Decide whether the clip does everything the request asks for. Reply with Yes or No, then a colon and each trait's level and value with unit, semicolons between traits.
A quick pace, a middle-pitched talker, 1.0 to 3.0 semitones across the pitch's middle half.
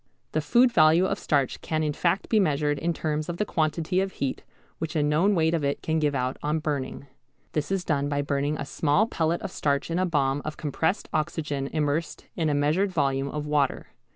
Yes: fast, 215 wpm; medium, 155 Hz; average, 2.7 semitones